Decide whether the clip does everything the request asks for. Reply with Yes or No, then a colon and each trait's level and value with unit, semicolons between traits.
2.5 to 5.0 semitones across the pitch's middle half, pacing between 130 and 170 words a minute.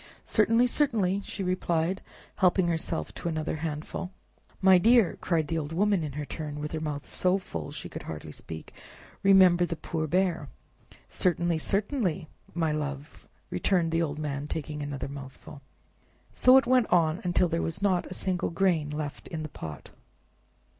Yes: average, 3.9 semitones; average, 165 wpm